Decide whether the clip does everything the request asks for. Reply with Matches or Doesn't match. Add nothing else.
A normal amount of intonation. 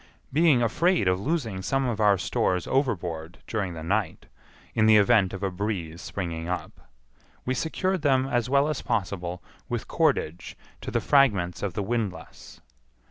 Doesn't match